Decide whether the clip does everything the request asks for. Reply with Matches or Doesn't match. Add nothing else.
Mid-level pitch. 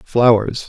Doesn't match